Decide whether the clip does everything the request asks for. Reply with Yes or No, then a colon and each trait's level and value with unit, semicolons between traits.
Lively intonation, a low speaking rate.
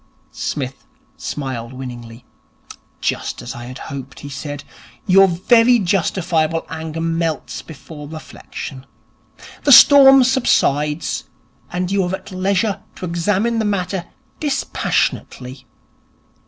Yes: wide, 5.9 semitones; slow, 110 wpm